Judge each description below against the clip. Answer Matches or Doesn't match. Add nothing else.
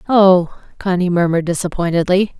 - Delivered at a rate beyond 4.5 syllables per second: Matches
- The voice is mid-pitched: Matches